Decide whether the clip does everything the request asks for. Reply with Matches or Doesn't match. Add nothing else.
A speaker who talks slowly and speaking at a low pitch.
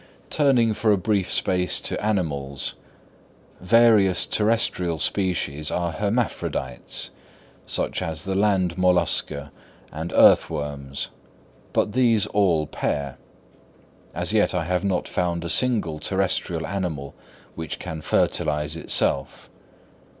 Matches